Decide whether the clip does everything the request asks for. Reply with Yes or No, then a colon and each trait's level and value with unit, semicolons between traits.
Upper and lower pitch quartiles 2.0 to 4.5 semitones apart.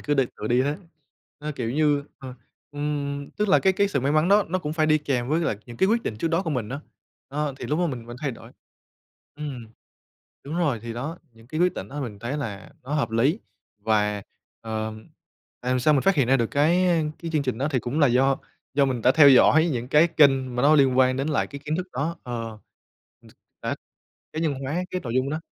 Yes: average, 4.1 semitones